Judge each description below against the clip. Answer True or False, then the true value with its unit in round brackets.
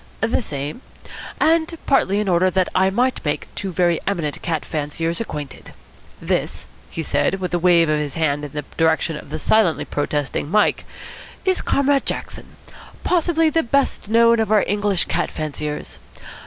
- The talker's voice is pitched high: False (180 Hz)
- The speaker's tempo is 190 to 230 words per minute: False (165 wpm)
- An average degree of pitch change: False (6.9 semitones)